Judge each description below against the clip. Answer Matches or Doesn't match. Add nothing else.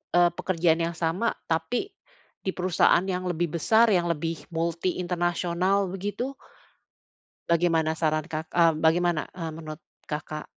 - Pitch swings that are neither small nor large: Doesn't match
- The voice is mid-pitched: Matches